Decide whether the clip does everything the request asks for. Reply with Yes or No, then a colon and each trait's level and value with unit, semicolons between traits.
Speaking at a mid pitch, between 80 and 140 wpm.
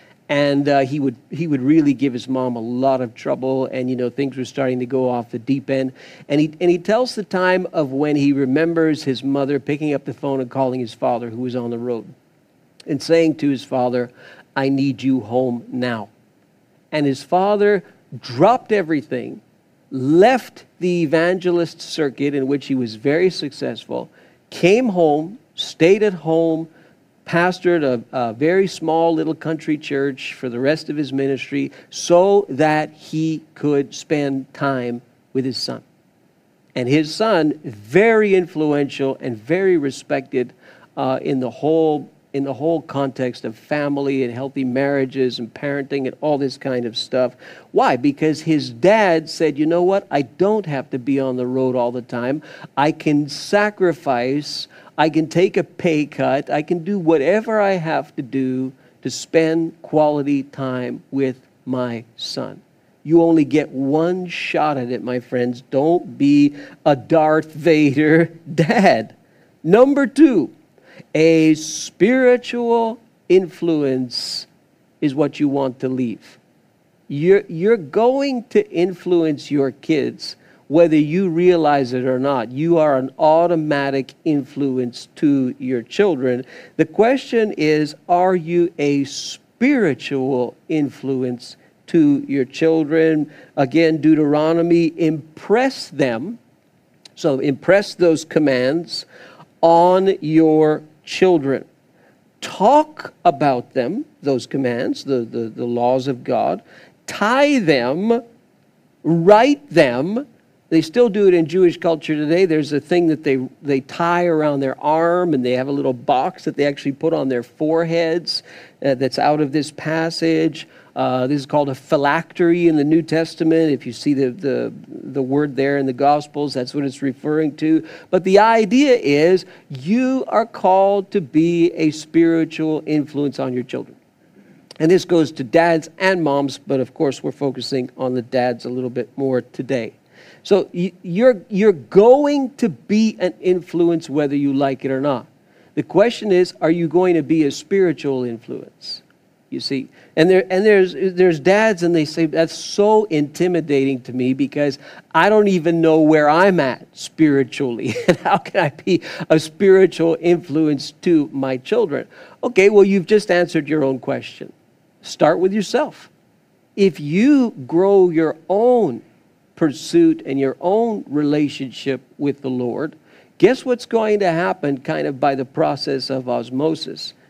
No: medium, 155 Hz; average, 155 wpm